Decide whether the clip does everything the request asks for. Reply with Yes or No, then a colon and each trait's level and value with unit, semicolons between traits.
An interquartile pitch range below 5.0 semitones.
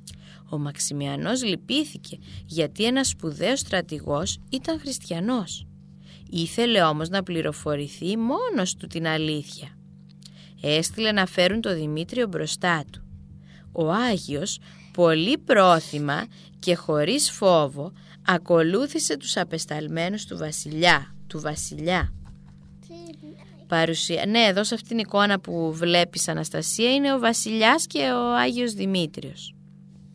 No: wide, 5.5 semitones